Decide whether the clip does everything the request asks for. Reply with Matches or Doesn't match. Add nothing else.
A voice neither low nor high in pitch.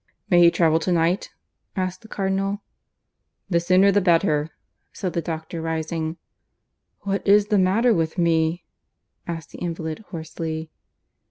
Matches